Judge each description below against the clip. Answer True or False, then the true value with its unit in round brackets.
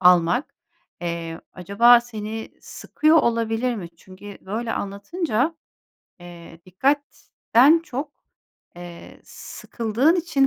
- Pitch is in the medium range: False (225 Hz)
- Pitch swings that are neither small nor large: False (6.8 semitones)